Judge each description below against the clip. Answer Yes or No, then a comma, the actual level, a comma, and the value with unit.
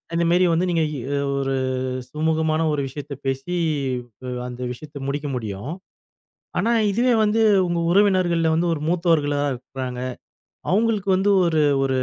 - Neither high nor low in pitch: Yes, medium, 160 Hz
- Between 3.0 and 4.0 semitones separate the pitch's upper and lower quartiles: No, average, 4.6 semitones